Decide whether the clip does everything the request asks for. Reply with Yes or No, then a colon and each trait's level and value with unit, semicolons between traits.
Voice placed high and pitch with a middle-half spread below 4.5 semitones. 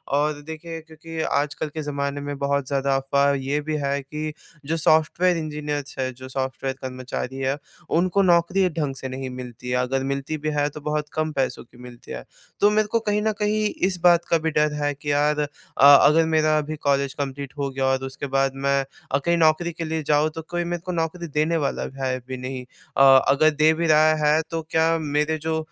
No: medium, 150 Hz; average, 2.9 semitones